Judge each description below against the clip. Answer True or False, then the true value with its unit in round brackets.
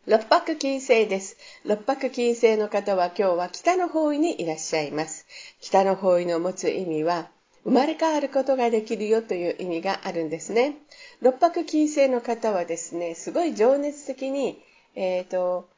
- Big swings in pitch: True (7.4 semitones)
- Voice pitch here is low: False (225 Hz)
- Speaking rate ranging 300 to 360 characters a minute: True (325 characters per minute)